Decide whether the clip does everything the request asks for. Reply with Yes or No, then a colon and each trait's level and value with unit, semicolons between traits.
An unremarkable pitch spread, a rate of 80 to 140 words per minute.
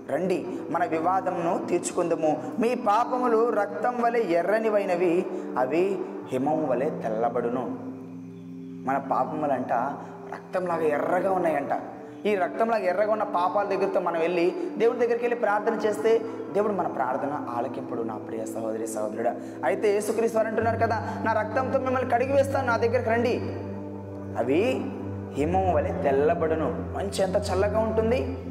No: wide, 6.3 semitones; average, 120 wpm